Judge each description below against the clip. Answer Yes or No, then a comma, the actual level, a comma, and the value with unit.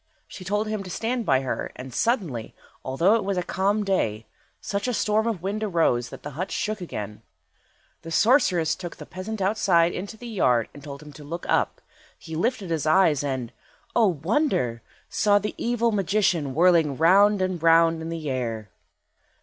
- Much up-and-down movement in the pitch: Yes, wide, 6.0 semitones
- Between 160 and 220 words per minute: Yes, average, 180 wpm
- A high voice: No, medium, 180 Hz